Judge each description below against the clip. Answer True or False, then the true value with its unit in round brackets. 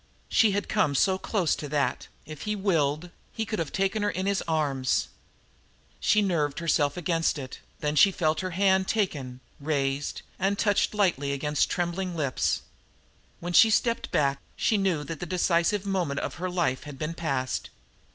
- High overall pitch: False (170 Hz)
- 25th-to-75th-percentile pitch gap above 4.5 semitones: True (4.9 semitones)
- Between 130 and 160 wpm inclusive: False (170 wpm)